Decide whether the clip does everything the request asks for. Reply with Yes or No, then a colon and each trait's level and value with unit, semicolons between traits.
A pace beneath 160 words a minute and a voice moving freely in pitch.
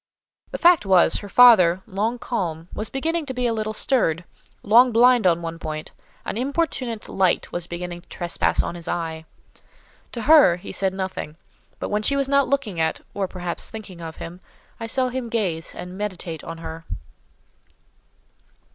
No: average, 170 wpm; wide, 6.1 semitones